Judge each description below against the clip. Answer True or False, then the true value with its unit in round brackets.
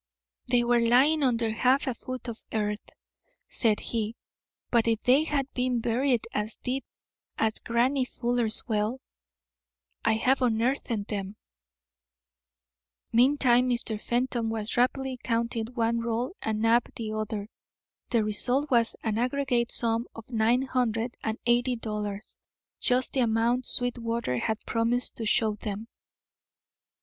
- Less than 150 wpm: True (135 wpm)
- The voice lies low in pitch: False (235 Hz)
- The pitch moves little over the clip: True (2.1 semitones)